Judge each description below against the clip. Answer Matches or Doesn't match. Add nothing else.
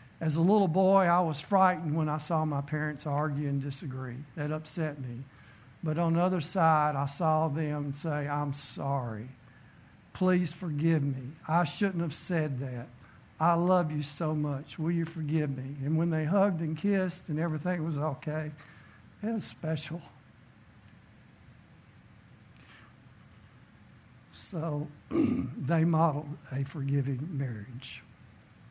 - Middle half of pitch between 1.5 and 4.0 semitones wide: Matches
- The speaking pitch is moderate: Matches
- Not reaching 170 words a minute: Matches